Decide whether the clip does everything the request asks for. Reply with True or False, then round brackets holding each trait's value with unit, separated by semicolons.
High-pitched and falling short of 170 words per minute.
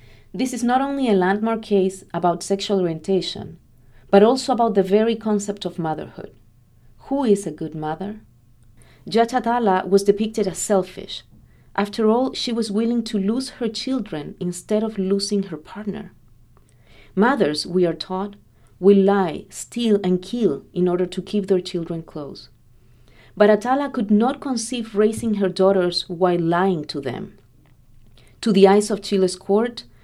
True (195 Hz; 150 wpm)